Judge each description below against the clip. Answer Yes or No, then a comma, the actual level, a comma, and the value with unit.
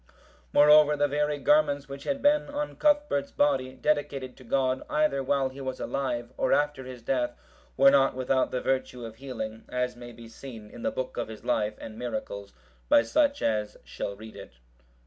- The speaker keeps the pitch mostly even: No, average, 3.4 semitones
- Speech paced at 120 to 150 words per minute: No, average, 185 wpm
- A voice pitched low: Yes, low, 130 Hz